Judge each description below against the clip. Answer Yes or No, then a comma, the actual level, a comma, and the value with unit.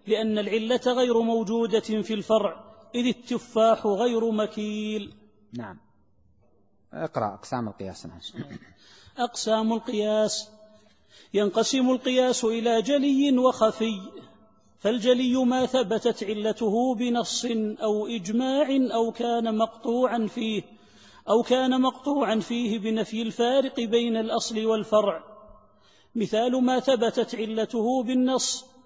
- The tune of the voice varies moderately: No, narrow, 2.3 semitones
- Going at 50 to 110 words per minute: Yes, average, 95 wpm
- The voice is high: Yes, high, 225 Hz